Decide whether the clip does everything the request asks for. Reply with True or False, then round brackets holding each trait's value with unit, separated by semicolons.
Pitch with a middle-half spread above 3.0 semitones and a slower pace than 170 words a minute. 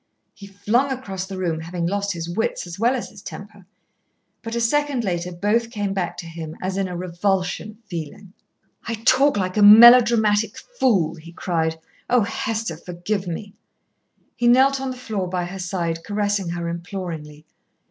False (4.5 semitones; 175 wpm)